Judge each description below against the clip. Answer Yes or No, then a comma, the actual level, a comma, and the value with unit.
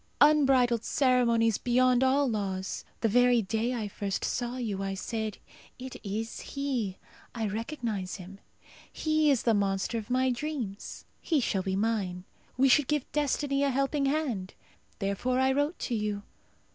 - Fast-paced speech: No, average, 155 wpm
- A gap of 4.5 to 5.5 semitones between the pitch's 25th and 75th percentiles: Yes, average, 4.8 semitones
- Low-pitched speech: No, high, 240 Hz